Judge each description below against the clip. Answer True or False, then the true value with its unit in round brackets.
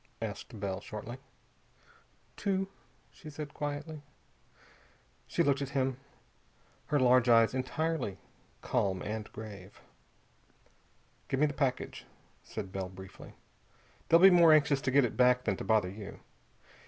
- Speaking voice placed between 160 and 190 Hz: False (130 Hz)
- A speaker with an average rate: False (130 wpm)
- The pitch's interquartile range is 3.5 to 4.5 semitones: False (5.6 semitones)